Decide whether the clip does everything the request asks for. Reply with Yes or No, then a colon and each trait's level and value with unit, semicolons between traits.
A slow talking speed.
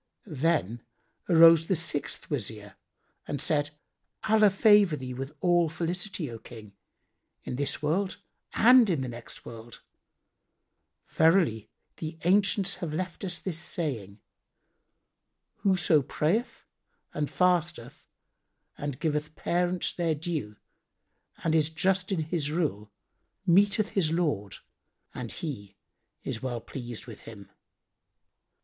Yes: slow, 115 wpm